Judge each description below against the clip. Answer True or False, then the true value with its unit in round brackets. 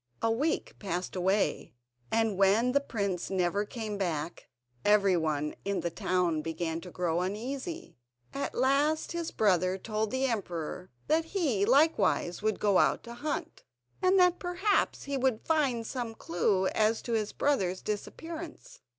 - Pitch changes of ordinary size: False (7.1 semitones)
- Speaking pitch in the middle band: False (215 Hz)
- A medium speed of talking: True (150 wpm)